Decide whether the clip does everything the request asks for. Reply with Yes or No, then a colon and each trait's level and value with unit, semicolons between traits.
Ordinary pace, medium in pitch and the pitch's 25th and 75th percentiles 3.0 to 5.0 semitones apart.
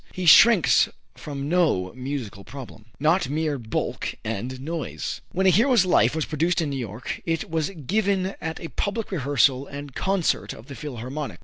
No: average, 170 wpm; medium, 150 Hz; wide, 5.4 semitones